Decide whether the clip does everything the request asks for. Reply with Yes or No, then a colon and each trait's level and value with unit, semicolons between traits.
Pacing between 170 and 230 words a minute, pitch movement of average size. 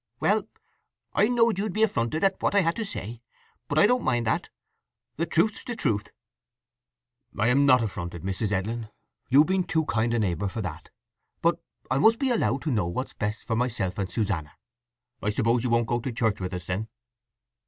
No: average, 195 wpm; wide, 8.2 semitones